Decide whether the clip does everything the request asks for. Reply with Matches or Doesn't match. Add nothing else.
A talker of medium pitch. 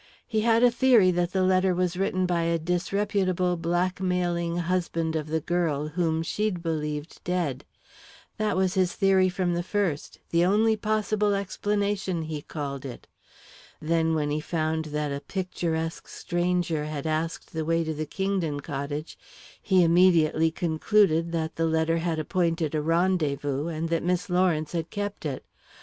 Matches